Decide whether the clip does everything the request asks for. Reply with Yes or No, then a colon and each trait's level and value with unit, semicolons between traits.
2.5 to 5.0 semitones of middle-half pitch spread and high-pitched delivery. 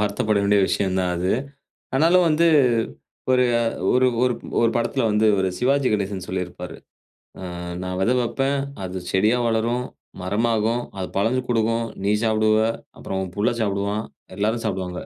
No: average, 3.7 semitones; low, 110 Hz